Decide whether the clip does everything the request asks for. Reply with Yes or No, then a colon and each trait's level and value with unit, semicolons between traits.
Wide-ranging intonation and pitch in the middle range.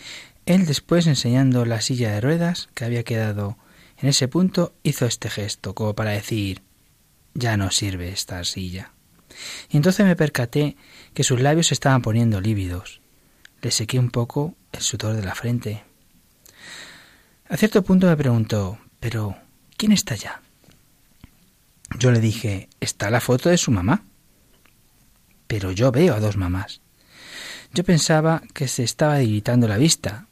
No: wide, 5.7 semitones; low, 120 Hz